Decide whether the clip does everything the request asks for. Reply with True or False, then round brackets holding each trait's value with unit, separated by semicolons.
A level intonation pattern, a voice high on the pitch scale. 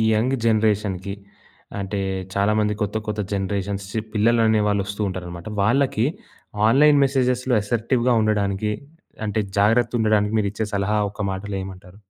False (2.2 semitones; 105 Hz)